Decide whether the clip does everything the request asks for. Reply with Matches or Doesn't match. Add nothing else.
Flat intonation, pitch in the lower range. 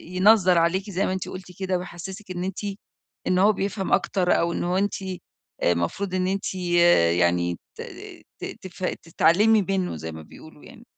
Doesn't match